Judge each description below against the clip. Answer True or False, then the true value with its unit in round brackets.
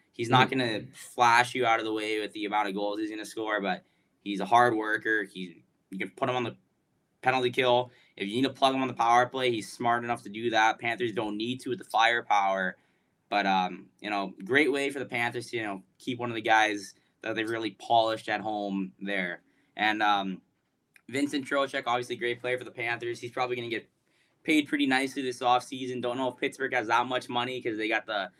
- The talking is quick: True (230 wpm)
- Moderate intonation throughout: True (3.0 semitones)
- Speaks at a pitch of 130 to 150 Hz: False (115 Hz)